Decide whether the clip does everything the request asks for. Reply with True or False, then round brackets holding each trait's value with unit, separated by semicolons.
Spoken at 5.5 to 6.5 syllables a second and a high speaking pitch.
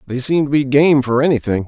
False (5.9 syllables/s; 135 Hz)